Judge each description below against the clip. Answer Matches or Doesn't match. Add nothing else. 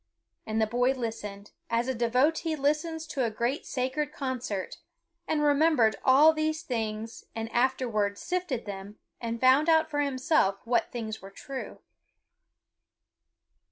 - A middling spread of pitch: Matches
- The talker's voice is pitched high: Matches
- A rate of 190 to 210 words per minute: Doesn't match